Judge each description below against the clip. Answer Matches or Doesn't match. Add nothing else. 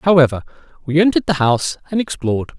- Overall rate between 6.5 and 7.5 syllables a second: Matches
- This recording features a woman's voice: Doesn't match